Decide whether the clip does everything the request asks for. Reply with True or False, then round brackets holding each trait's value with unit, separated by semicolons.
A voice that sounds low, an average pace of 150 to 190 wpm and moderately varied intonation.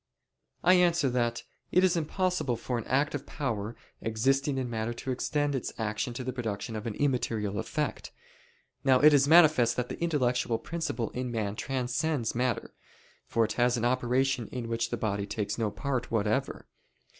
True (125 Hz; 170 wpm; 3.5 semitones)